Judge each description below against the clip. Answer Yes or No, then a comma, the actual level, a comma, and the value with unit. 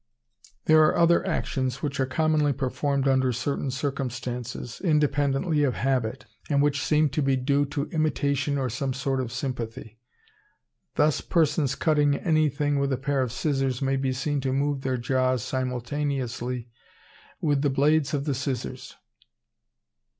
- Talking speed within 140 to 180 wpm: Yes, average, 150 wpm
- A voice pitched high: No, low, 135 Hz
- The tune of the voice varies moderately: No, narrow, 2.2 semitones